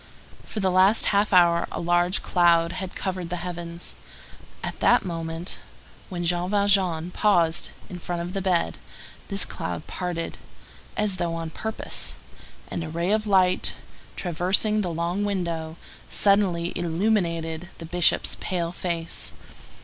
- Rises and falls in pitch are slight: Yes, narrow, 2.2 semitones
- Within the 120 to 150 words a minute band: Yes, average, 140 wpm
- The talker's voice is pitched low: No, medium, 175 Hz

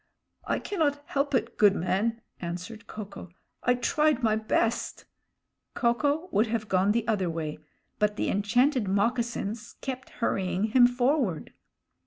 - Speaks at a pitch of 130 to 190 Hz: No, high, 225 Hz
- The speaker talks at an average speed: Yes, average, 150 wpm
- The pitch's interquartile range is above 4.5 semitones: No, average, 3.9 semitones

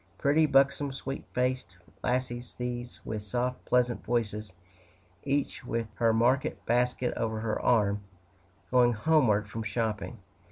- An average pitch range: No, narrow, 2.3 semitones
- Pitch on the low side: Yes, low, 120 Hz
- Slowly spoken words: Yes, slow, 125 wpm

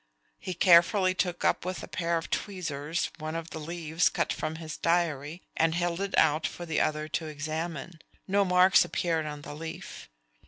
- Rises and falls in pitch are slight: Yes, narrow, 2.3 semitones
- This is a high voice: No, medium, 165 Hz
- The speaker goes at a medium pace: Yes, average, 185 wpm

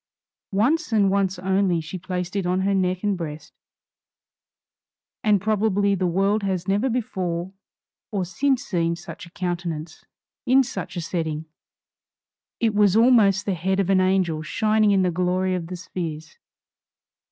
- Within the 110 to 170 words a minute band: Yes, average, 150 wpm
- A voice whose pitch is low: No, high, 190 Hz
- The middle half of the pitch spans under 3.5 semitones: Yes, narrow, 2.6 semitones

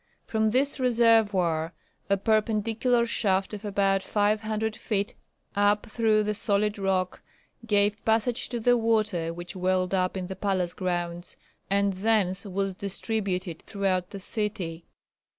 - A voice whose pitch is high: Yes, high, 200 Hz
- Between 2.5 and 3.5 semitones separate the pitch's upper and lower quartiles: Yes, average, 2.8 semitones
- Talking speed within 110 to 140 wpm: Yes, slow, 135 wpm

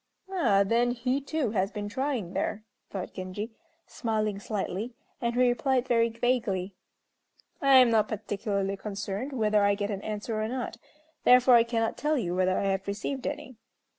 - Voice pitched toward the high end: Yes, high, 220 Hz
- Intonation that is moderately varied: Yes, average, 3.7 semitones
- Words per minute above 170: No, average, 165 wpm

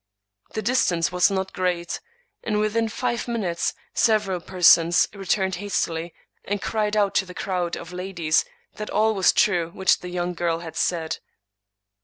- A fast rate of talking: No, average, 155 wpm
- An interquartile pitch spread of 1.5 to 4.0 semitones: Yes, average, 3.3 semitones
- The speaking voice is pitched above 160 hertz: Yes, medium, 185 Hz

